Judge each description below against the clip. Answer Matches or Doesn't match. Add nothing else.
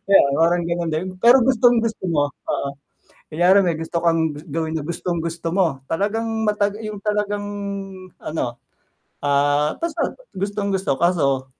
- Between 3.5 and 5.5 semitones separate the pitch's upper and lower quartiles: Matches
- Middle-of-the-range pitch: Matches